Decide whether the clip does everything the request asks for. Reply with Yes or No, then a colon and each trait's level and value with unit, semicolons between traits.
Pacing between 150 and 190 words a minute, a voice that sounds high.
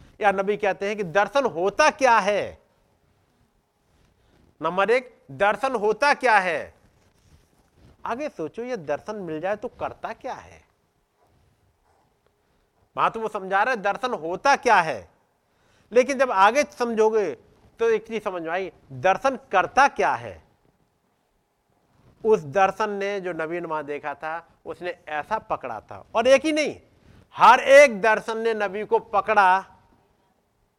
No: average, 135 wpm; high, 205 Hz